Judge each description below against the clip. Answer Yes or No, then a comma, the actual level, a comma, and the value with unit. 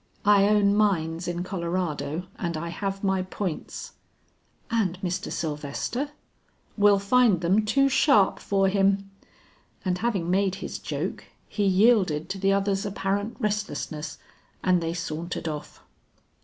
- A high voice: Yes, high, 195 Hz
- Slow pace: Yes, slow, 130 wpm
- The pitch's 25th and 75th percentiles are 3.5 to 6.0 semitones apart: No, average, 3.0 semitones